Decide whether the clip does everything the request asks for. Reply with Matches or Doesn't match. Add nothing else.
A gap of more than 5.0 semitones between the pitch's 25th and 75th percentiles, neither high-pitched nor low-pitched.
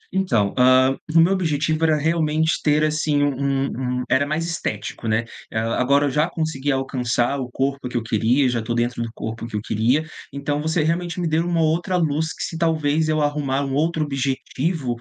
Doesn't match